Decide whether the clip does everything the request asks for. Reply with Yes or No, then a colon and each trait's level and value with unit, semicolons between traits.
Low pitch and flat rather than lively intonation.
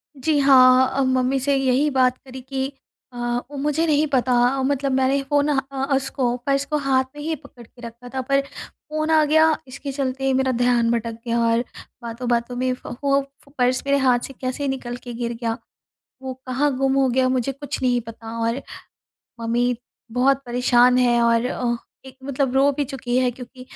No: very high, 260 Hz; narrow, 2.1 semitones